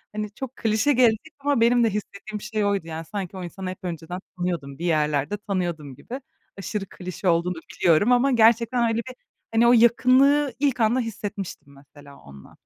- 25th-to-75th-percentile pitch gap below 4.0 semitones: No, wide, 5.5 semitones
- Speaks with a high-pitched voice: Yes, high, 205 Hz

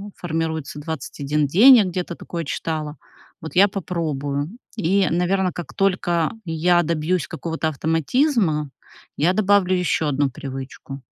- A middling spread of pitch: Yes, average, 3.3 semitones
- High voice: No, medium, 165 Hz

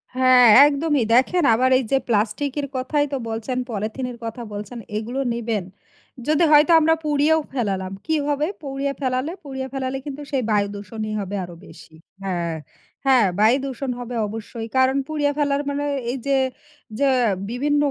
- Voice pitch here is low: No, very high, 260 Hz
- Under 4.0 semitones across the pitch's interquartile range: No, average, 4.3 semitones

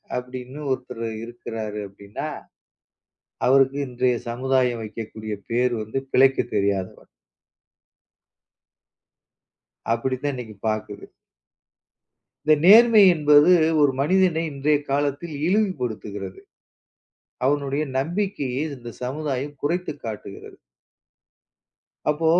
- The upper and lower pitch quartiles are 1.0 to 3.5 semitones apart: No, average, 4.2 semitones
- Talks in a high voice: No, low, 130 Hz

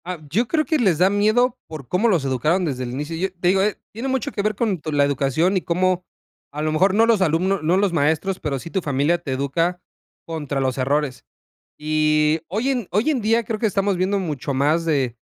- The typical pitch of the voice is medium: Yes, medium, 175 Hz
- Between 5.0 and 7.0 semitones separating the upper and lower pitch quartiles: Yes, average, 5.3 semitones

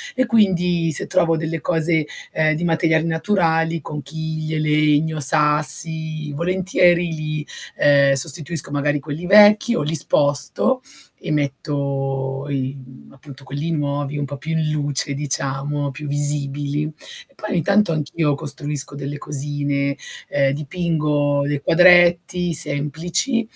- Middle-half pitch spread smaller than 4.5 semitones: Yes, narrow, 2.6 semitones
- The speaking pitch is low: No, medium, 150 Hz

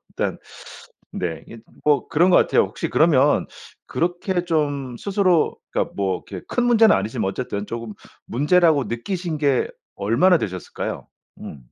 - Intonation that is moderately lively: No, wide, 8.0 semitones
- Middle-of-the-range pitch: Yes, medium, 145 Hz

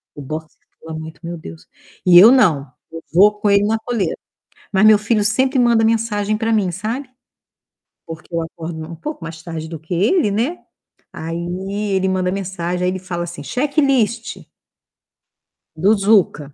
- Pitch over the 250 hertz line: No, high, 190 Hz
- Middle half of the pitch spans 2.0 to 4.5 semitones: No, average, 5.0 semitones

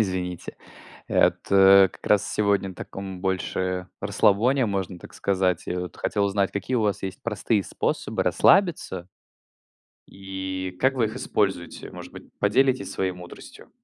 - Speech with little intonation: Yes, narrow, 2.1 semitones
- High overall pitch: No, very low, 95 Hz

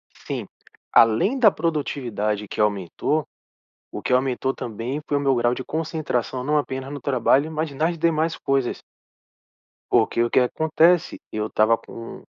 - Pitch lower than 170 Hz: Yes, low, 135 Hz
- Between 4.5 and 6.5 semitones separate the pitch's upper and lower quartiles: Yes, average, 4.8 semitones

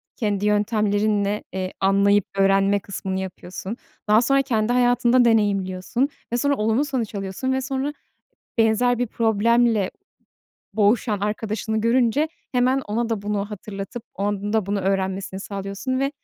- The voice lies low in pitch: No, high, 210 Hz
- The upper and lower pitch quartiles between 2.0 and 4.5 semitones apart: Yes, average, 3.3 semitones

